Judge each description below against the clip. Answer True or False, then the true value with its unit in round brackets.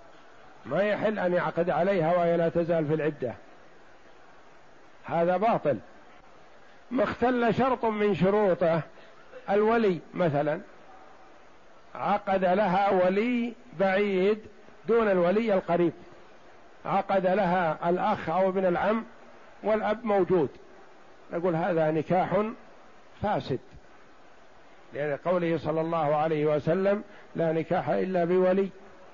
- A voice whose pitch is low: False (185 Hz)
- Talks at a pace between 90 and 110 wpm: True (100 wpm)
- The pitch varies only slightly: False (3.5 semitones)